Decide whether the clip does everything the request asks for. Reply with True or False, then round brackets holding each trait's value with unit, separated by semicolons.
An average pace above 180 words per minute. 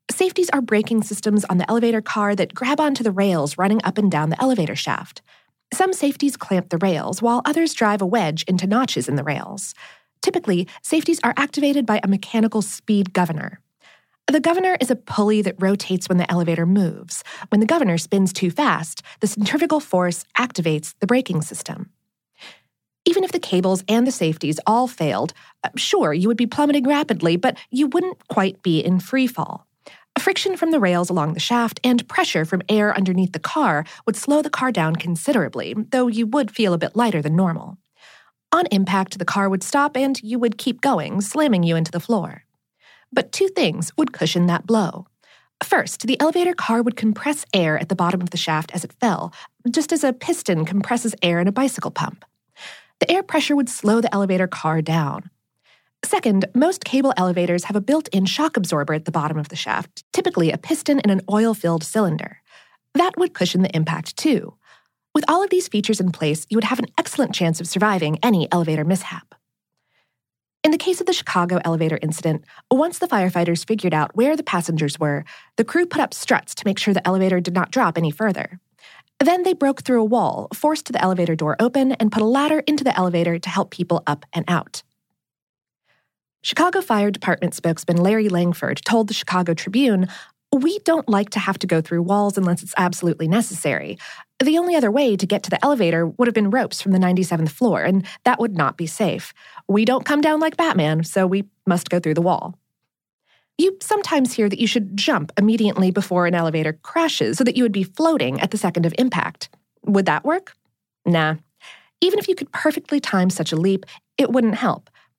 True (200 wpm)